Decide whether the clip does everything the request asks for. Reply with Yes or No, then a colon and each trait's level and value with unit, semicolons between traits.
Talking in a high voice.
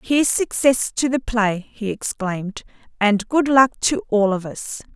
Yes: high, 235 Hz